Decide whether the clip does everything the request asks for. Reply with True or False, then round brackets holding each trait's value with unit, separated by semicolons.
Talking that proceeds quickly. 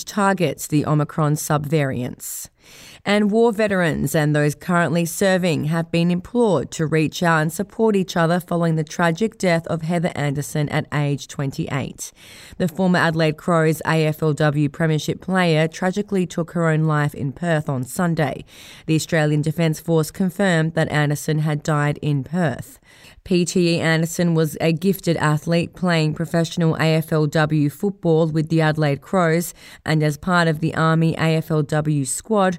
False (145 wpm)